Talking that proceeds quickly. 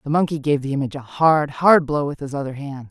Yes: fast, 270 wpm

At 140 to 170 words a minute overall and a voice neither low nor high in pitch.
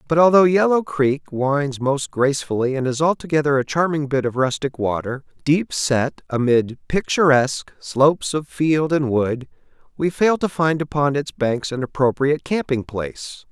Yes: average, 160 wpm; medium, 145 Hz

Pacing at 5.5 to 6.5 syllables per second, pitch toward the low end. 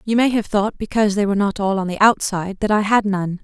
No: 6.4 syllables/s; high, 205 Hz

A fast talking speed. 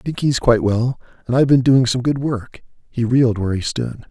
Yes: fast, 220 wpm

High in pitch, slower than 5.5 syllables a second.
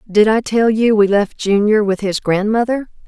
Yes: high, 210 Hz; 4.8 syllables/s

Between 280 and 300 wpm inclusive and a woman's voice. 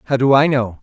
No: fast, 290 wpm; male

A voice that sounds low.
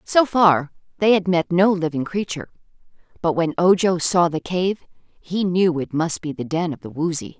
No: medium, 175 Hz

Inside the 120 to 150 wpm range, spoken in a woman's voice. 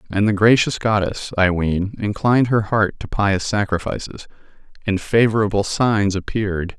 No: average, 140 wpm; male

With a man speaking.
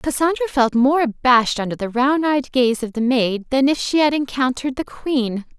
No: female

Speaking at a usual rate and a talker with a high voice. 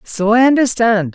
Yes: average, 155 wpm; high, 225 Hz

